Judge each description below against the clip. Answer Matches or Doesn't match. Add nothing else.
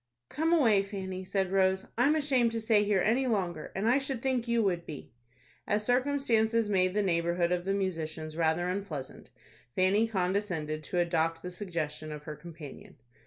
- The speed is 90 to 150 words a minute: Doesn't match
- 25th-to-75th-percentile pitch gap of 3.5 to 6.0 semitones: Matches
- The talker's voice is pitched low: Doesn't match